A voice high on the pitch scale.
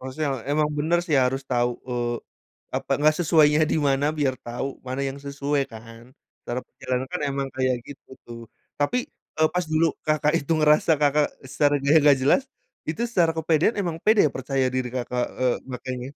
No: medium, 140 Hz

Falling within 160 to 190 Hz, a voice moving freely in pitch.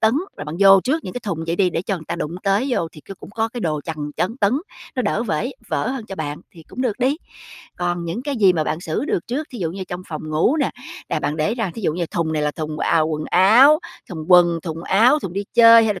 Yes: medium, 185 Hz; wide, 6.0 semitones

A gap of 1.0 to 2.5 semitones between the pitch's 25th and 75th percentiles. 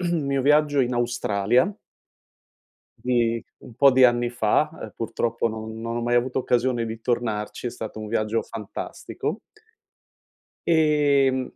No: average, 2.9 semitones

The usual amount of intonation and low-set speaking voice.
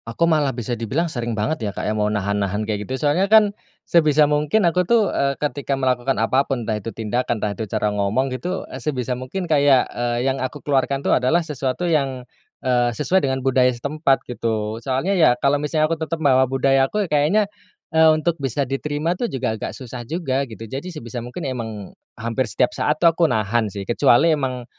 Yes: average, 4.4 semitones; low, 130 Hz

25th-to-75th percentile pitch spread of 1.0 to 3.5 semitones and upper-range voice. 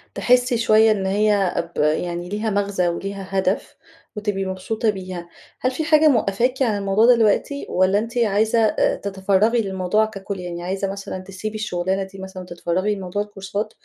Yes: narrow, 2.5 semitones; high, 200 Hz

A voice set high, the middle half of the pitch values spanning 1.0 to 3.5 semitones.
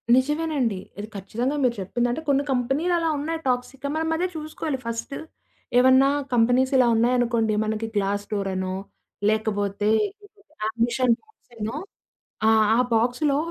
No: high, 245 Hz; average, 4.1 semitones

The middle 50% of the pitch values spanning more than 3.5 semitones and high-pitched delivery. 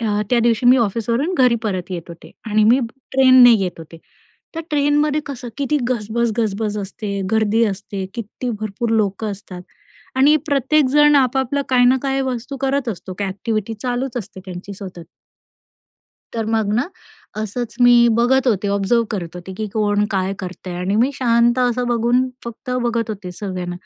Yes: average, 4.0 semitones; high, 230 Hz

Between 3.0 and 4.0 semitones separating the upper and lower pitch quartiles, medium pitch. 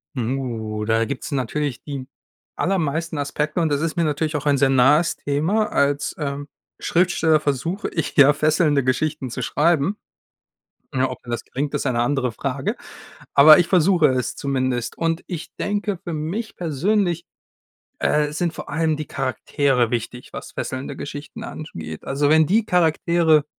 Yes: average, 3.7 semitones; medium, 150 Hz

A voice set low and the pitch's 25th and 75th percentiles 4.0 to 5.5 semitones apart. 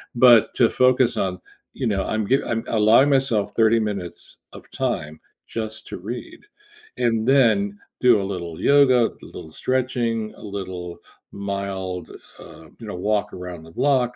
Yes: low, 110 Hz; average, 4.5 semitones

